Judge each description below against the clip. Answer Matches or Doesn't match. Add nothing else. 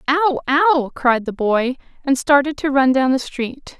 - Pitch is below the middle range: Doesn't match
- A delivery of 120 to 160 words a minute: Doesn't match